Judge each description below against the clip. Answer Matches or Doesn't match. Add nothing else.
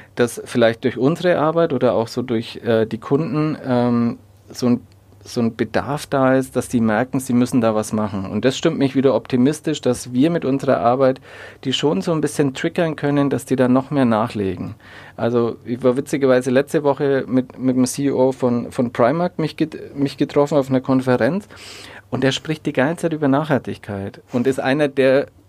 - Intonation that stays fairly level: Doesn't match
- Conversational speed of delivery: Doesn't match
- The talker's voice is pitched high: Doesn't match